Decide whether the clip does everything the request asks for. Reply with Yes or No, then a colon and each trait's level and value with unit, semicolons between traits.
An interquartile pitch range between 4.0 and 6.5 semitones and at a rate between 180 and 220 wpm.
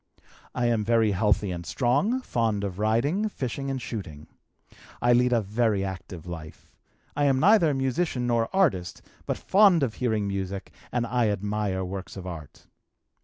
No: average, 5.1 semitones; average, 160 wpm